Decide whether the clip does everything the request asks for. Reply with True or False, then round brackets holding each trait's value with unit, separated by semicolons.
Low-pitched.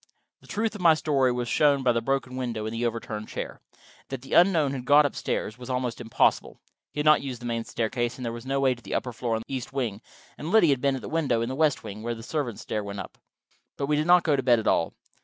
True (130 Hz)